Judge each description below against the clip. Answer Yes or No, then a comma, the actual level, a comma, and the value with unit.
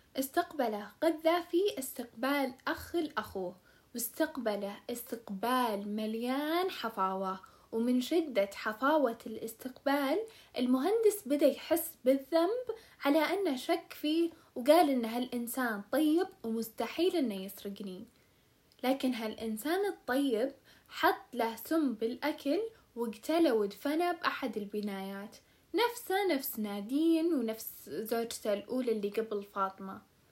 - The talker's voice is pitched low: No, very high, 260 Hz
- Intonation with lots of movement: Yes, wide, 6.4 semitones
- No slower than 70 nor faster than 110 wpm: Yes, average, 95 wpm